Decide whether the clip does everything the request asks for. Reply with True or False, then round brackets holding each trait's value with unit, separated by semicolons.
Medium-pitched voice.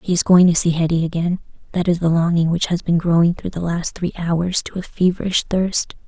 True (170 Hz)